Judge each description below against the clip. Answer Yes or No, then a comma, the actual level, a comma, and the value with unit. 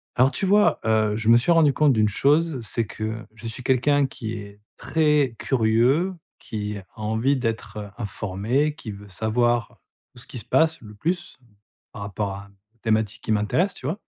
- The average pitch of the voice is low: Yes, low, 115 Hz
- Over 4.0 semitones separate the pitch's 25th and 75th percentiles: Yes, average, 5.0 semitones